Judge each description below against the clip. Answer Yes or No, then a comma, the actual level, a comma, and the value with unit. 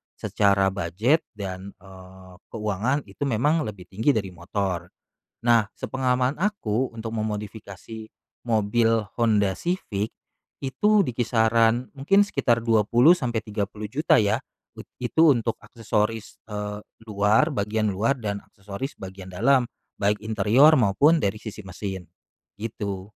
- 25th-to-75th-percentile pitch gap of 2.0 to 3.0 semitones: No, average, 3.7 semitones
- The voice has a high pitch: No, low, 110 Hz